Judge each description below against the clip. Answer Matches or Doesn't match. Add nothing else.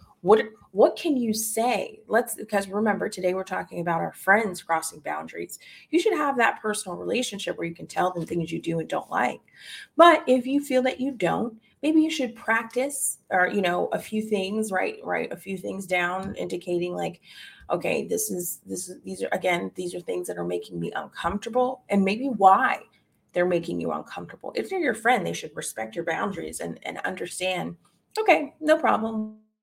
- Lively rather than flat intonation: Matches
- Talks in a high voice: Matches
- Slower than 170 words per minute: Doesn't match